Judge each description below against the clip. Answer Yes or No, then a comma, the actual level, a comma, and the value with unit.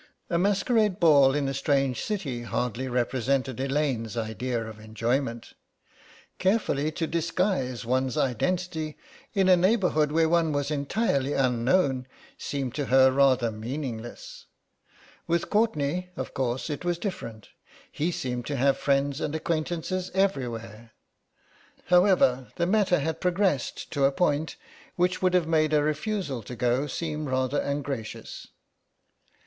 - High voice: No, medium, 140 Hz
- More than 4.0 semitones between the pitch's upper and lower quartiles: Yes, average, 5.1 semitones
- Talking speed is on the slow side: Yes, slow, 130 wpm